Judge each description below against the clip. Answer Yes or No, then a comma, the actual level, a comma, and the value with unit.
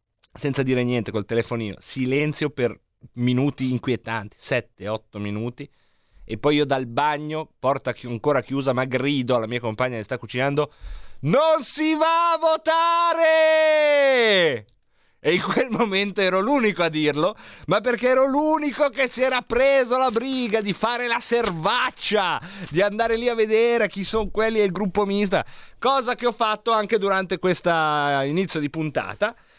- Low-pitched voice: No, high, 190 Hz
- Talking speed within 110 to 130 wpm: No, average, 160 wpm